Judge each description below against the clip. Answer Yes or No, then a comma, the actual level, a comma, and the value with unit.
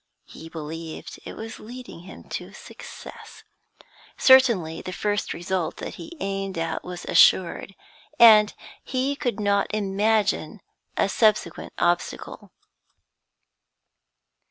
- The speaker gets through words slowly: Yes, slow, 110 wpm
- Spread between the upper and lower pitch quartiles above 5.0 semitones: No, average, 4.2 semitones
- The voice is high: Yes, high, 200 Hz